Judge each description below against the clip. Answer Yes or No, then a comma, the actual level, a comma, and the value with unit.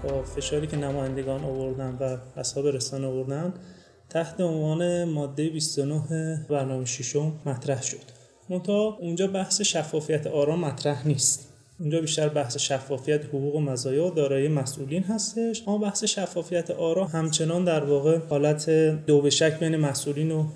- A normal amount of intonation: Yes, average, 3.0 semitones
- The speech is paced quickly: No, average, 140 wpm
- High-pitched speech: No, medium, 150 Hz